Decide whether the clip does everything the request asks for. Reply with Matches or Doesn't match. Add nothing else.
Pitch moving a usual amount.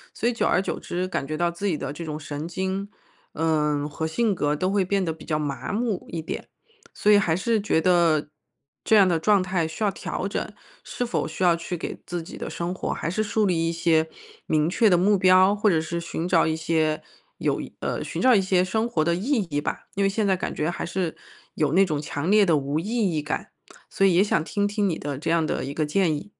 Matches